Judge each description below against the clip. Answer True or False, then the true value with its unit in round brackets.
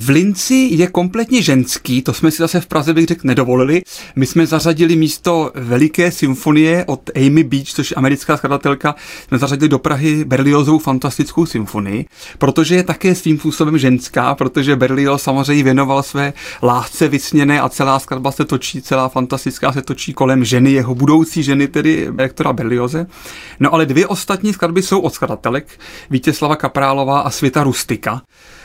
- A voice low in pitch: False (145 Hz)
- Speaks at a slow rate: False (160 wpm)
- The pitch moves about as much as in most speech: True (3.2 semitones)